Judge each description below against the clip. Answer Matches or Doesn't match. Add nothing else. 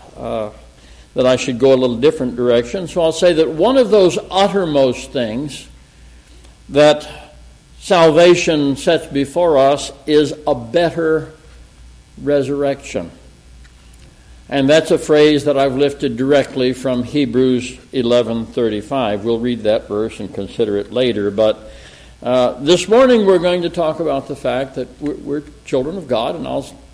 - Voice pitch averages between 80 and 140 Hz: Matches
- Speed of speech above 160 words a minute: Doesn't match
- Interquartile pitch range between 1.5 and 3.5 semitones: Doesn't match